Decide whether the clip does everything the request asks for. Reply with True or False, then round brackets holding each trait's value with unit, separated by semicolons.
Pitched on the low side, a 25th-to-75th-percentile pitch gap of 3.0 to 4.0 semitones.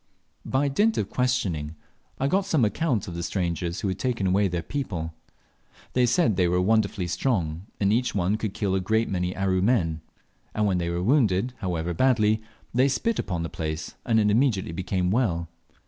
False (100 Hz; 5.6 semitones)